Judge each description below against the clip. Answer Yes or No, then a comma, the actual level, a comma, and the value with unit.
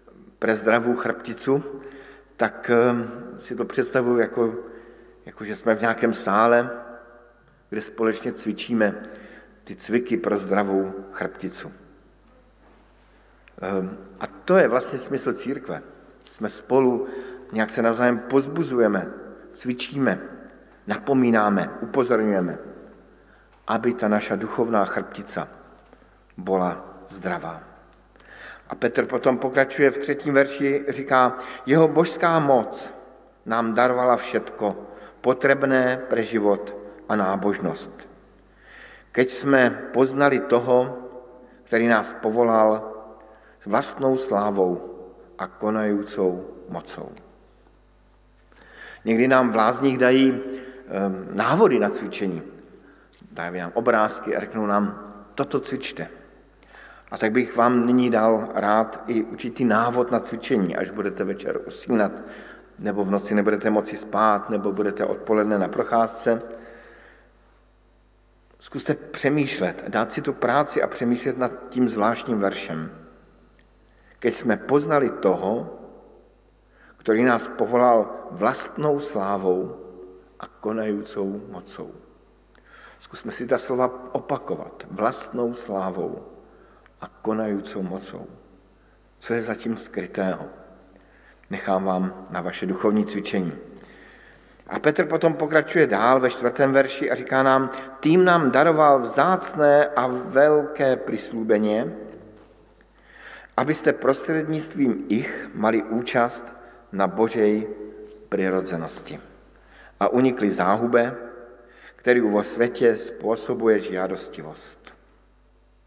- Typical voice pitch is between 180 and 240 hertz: No, low, 115 Hz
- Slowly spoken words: Yes, slow, 100 wpm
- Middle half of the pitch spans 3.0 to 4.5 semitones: Yes, average, 3.6 semitones